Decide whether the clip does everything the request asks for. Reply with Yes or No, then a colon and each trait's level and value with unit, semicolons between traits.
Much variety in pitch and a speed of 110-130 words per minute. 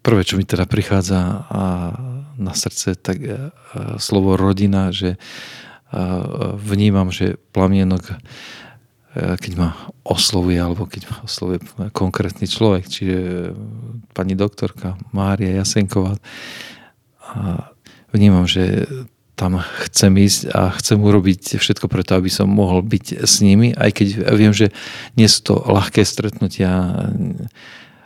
No: narrow, 2.5 semitones; average, 115 wpm